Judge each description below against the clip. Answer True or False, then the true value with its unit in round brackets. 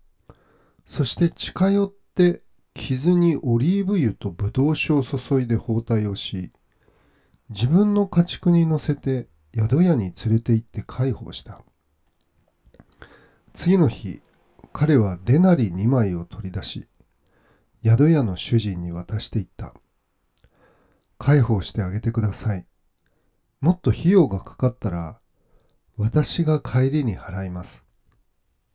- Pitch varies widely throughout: True (7.6 semitones)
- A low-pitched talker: True (115 Hz)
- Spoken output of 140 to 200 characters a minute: False (220 characters per minute)